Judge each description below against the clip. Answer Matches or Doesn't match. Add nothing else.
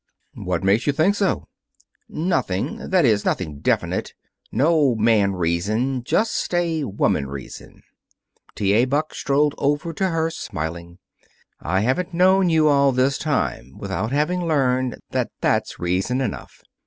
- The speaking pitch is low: Matches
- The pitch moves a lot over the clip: Matches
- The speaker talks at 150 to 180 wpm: Doesn't match